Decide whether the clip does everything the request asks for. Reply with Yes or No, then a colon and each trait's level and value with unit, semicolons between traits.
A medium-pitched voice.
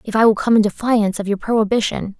No: high, 215 Hz